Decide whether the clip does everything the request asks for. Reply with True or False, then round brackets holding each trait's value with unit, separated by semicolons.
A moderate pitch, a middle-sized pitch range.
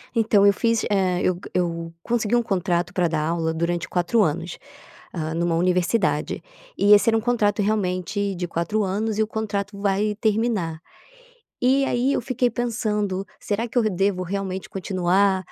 False (200 Hz; 3.7 semitones)